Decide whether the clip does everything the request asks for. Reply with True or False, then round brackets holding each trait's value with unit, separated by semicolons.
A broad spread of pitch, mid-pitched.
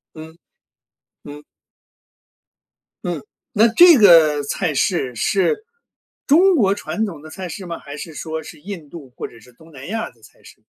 True (5.7 semitones; 165 Hz)